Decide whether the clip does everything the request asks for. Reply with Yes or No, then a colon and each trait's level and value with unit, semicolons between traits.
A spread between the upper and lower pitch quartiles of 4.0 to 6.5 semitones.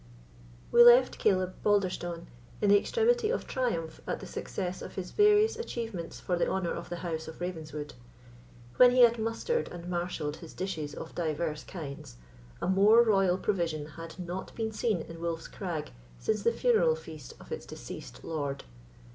Yes: wide, 5.6 semitones